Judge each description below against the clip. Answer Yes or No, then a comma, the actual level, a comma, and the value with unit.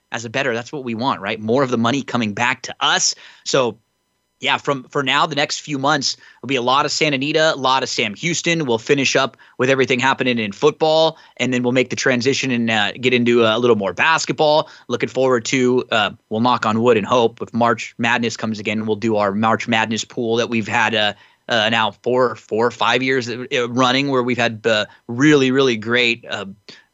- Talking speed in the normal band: No, fast, 225 wpm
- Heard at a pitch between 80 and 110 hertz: No, low, 125 Hz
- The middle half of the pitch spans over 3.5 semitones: No, average, 3.2 semitones